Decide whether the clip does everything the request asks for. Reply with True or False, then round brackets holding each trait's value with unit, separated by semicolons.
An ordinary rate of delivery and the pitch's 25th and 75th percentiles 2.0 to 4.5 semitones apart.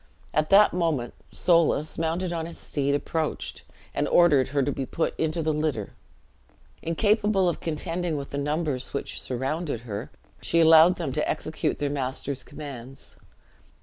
True (150 wpm; 3.2 semitones)